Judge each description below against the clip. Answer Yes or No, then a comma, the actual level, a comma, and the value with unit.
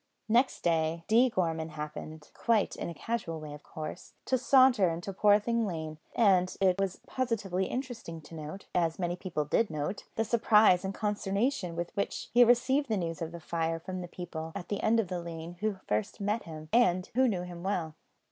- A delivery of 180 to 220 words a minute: Yes, average, 195 wpm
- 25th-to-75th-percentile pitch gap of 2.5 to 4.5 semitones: No, average, 4.9 semitones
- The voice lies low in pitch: No, medium, 185 Hz